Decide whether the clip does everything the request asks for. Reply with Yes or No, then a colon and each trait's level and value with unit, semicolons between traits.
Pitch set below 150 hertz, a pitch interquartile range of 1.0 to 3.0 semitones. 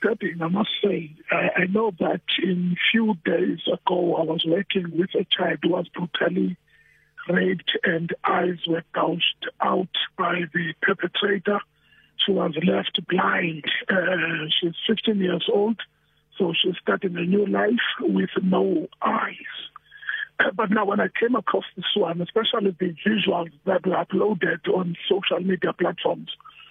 No: medium, 180 Hz; average, 2.7 semitones